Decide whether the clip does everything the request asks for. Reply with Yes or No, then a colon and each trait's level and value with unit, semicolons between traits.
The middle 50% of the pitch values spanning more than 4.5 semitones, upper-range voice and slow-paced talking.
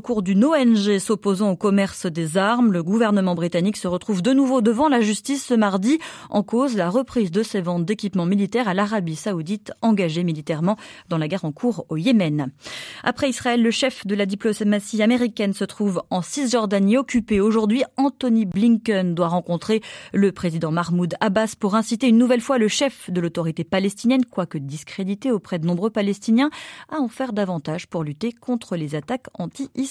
No: average, 4.9 semitones; high, 210 Hz; average, 185 wpm